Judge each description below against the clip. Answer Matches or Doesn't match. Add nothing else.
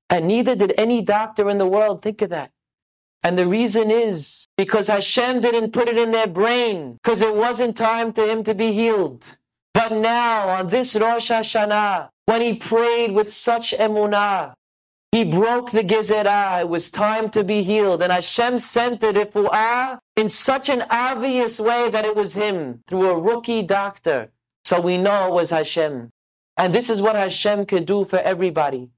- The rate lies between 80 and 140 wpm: Doesn't match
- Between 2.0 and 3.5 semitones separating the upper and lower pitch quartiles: Matches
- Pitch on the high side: Matches